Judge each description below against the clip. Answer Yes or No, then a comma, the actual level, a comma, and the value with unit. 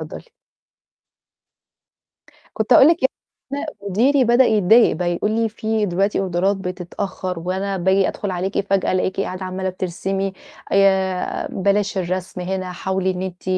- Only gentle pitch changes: Yes, narrow, 1.8 semitones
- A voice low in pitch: No, high, 190 Hz